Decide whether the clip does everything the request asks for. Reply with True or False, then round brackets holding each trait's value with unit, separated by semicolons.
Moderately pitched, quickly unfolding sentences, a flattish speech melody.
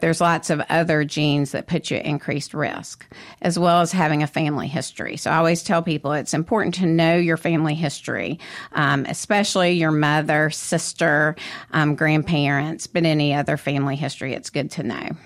False (155 Hz; 180 wpm; 2.2 semitones)